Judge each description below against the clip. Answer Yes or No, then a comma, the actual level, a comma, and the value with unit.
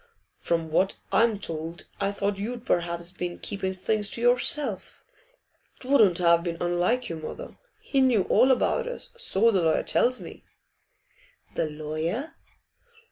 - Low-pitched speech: No, high, 195 Hz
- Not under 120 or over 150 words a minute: Yes, average, 140 wpm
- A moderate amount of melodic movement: No, wide, 6.0 semitones